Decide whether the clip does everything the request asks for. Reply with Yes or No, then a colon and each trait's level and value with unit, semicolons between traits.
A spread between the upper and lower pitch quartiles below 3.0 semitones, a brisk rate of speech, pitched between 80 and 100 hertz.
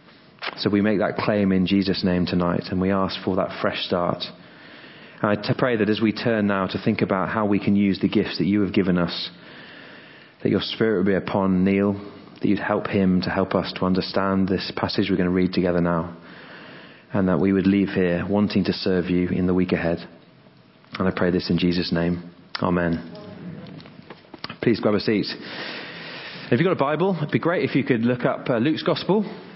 Yes: narrow, 2.5 semitones; fast, 210 wpm; very low, 95 Hz